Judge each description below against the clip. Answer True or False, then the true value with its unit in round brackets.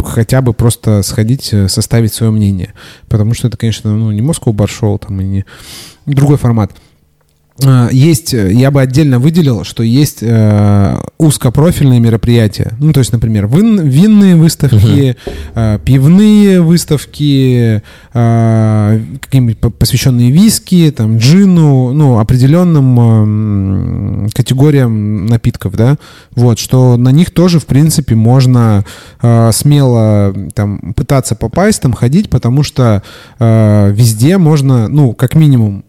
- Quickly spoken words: False (115 wpm)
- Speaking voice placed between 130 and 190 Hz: False (120 Hz)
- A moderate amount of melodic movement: True (4.6 semitones)